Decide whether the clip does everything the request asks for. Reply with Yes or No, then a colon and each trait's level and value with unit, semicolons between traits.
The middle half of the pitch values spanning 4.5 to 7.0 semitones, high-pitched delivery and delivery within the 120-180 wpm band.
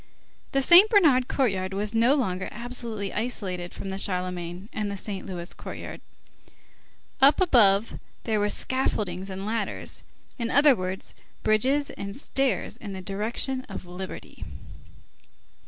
Yes: average, 5.1 semitones; high, 210 Hz; slow, 135 wpm